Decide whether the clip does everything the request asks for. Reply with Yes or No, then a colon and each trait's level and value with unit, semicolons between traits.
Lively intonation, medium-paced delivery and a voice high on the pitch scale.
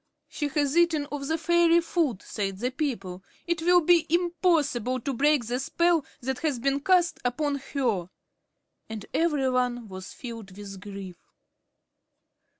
Yes: wide, 6.1 semitones; average, 150 wpm; very high, 275 Hz